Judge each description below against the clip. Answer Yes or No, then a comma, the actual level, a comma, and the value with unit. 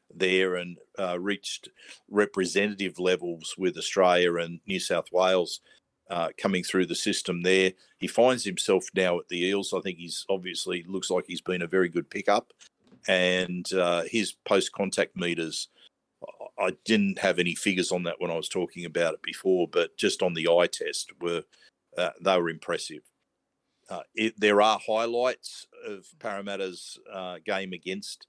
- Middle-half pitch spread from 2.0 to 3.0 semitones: No, average, 3.5 semitones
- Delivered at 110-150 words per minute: No, average, 165 wpm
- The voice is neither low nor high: No, very low, 95 Hz